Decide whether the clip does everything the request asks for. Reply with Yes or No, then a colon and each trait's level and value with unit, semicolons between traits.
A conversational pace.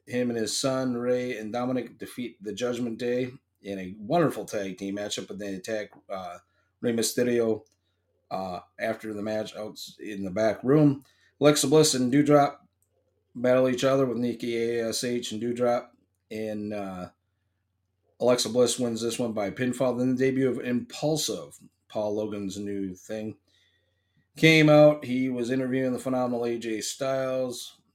Yes: average, 150 wpm